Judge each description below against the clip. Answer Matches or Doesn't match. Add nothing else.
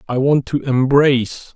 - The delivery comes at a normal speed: Matches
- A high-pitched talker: Doesn't match